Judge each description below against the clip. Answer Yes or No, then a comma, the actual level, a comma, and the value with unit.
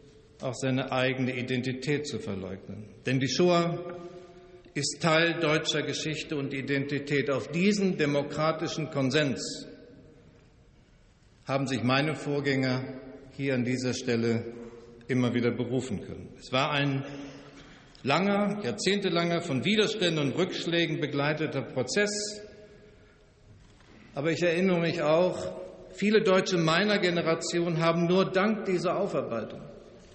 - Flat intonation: No, average, 5.1 semitones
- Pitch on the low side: No, medium, 145 Hz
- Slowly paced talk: Yes, slow, 110 wpm